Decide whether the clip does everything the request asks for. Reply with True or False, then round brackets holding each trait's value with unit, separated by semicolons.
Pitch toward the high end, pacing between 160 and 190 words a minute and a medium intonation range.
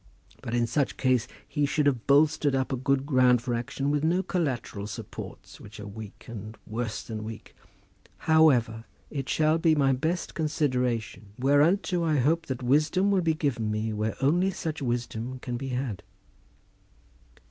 False (130 Hz; 165 wpm; 4.8 semitones)